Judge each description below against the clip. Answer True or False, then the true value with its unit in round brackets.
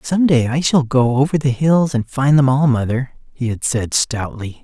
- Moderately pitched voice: False (130 Hz)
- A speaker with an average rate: False (220 wpm)